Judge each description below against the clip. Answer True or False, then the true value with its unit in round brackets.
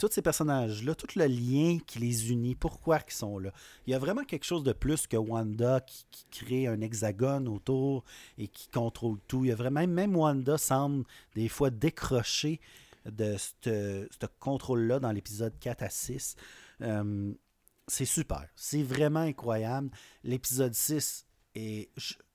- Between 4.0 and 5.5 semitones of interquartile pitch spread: True (4.3 semitones)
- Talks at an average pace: True (165 wpm)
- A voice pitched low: True (125 Hz)